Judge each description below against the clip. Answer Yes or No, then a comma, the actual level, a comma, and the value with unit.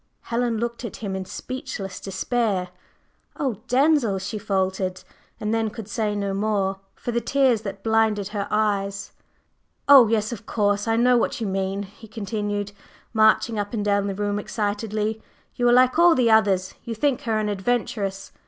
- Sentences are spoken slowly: No, average, 170 wpm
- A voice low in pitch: No, high, 215 Hz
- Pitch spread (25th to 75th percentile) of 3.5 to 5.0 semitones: No, average, 2.7 semitones